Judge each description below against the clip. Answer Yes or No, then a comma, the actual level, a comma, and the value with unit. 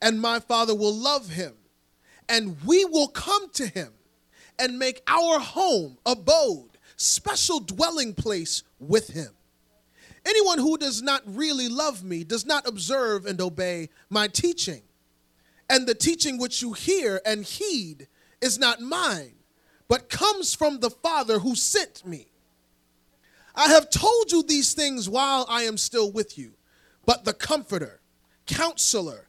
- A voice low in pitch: No, high, 235 Hz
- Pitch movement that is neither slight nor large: No, wide, 9.0 semitones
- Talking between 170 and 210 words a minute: No, average, 145 wpm